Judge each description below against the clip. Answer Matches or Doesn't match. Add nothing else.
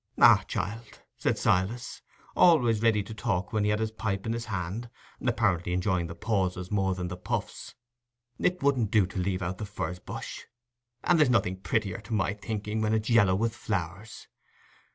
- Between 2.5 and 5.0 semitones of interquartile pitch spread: Matches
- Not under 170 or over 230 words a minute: Matches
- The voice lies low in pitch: Matches